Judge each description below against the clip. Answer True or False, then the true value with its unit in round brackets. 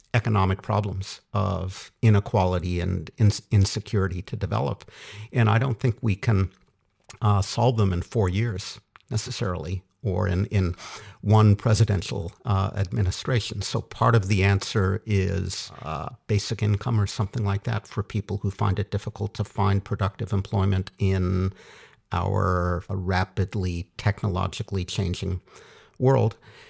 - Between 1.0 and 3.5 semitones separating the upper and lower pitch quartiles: True (2.7 semitones)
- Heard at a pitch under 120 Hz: True (100 Hz)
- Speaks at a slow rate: True (130 wpm)